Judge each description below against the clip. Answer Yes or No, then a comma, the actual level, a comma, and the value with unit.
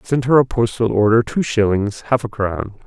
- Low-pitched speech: Yes, low, 115 Hz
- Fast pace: Yes, fast, 210 wpm